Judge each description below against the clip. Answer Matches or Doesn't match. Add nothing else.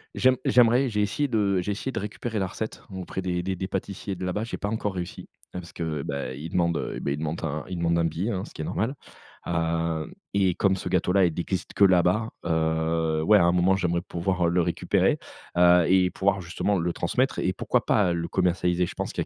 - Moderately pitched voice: Doesn't match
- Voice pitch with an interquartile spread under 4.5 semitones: Matches